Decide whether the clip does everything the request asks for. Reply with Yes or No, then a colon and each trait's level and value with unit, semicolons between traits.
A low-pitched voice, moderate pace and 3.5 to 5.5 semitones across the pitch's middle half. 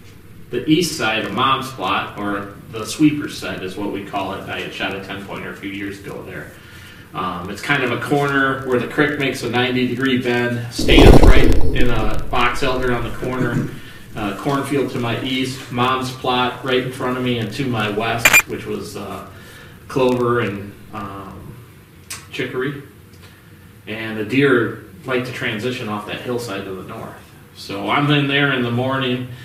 Yes: low, 120 Hz; average, 185 wpm; average, 4.3 semitones